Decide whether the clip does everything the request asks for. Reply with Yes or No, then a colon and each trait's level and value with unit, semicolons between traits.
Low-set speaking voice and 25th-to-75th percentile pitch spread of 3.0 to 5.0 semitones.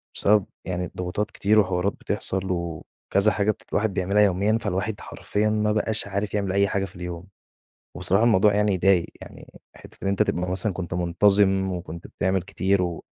No: very low, 95 Hz; narrow, 2.4 semitones